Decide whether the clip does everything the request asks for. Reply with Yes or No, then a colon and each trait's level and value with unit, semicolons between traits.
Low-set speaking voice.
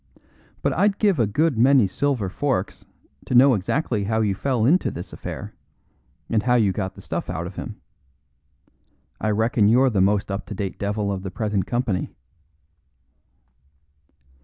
Yes: low, 110 Hz